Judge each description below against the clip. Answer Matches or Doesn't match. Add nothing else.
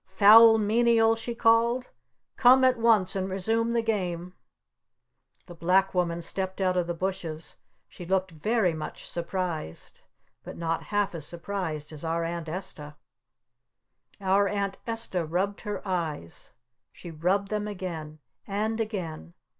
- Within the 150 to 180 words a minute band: Doesn't match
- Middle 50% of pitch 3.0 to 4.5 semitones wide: Matches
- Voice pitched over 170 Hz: Matches